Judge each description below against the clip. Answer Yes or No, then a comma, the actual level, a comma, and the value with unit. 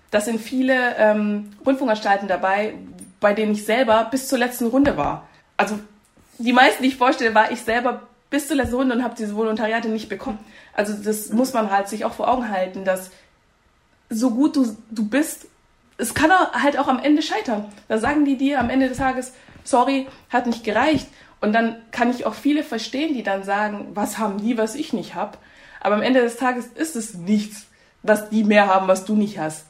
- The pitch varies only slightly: No, average, 3.7 semitones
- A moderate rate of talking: No, fast, 205 wpm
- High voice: Yes, high, 230 Hz